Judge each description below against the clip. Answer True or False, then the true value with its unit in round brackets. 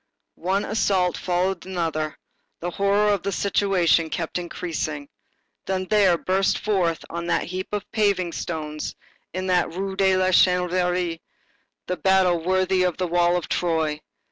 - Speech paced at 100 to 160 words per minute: True (145 wpm)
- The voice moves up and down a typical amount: False (1.9 semitones)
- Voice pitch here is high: False (180 Hz)